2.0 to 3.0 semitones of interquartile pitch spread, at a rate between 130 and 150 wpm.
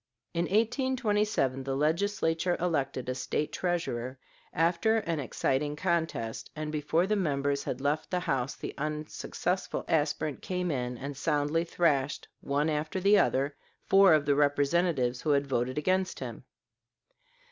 No: average, 4.2 semitones; average, 140 wpm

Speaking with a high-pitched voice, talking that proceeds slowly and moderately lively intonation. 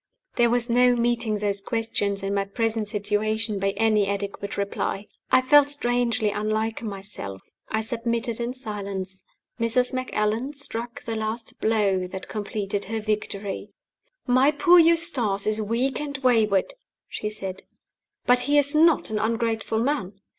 No: high, 220 Hz; average, 145 wpm; average, 3.2 semitones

